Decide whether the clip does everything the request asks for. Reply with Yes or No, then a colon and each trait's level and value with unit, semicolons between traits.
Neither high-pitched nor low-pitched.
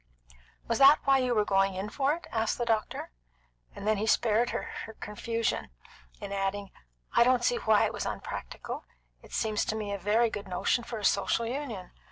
No: high, 220 Hz